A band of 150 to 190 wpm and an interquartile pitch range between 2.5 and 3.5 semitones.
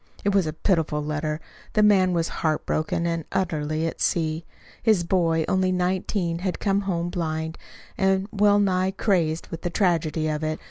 Yes: average, 175 wpm; average, 3.2 semitones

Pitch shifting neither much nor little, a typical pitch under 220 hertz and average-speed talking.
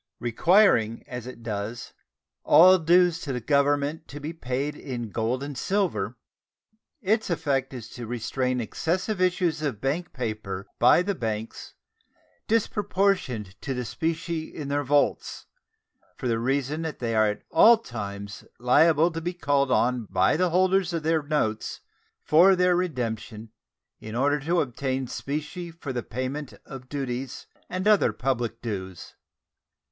No: wide, 5.9 semitones; medium, 140 Hz; average, 145 wpm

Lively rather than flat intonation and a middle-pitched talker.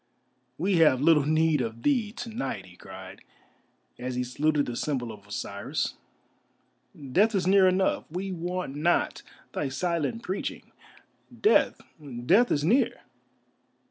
Yes: wide, 6.9 semitones; medium, 155 Hz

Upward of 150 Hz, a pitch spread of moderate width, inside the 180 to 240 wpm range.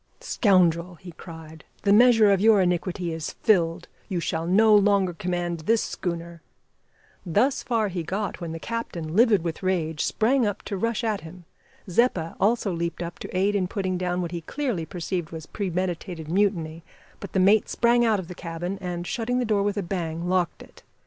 Yes: medium, 185 Hz; average, 3.5 semitones; average, 190 wpm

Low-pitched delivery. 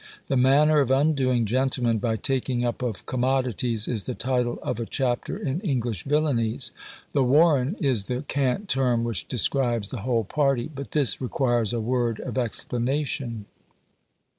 Yes: low, 125 Hz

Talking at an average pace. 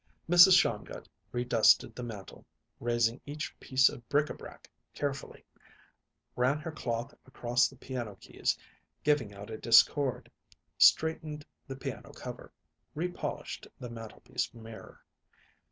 No: slow, 120 wpm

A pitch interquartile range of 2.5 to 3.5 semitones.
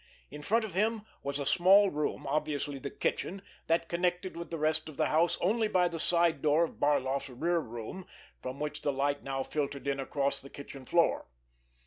No: average, 3.9 semitones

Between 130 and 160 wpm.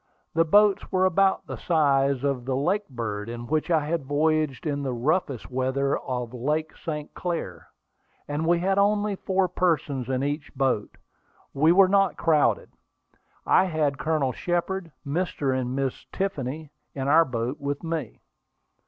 Yes: average, 155 wpm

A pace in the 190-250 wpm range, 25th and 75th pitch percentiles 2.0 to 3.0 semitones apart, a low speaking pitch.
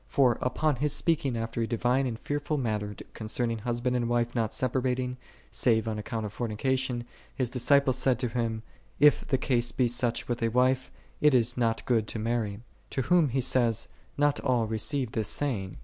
Yes: average, 200 wpm; narrow, 2.5 semitones; low, 120 Hz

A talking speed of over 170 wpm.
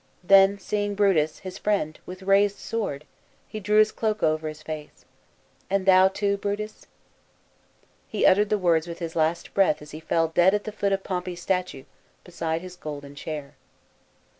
Yes: average, 180 wpm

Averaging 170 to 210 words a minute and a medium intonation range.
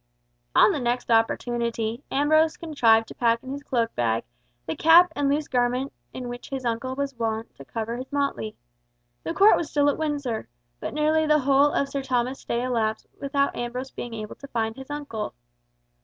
Yes: average, 185 wpm; average, 3.8 semitones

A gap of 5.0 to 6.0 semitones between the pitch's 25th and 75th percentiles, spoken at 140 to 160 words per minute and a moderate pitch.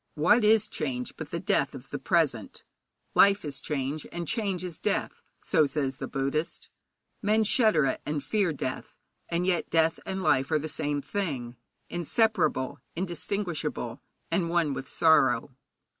Yes: average, 5.3 semitones; average, 155 wpm; medium, 160 Hz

